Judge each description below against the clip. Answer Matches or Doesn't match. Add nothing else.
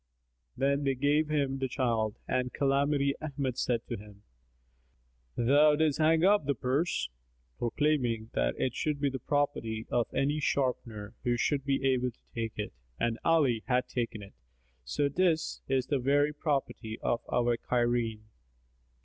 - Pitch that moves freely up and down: Doesn't match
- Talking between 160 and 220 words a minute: Doesn't match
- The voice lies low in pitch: Matches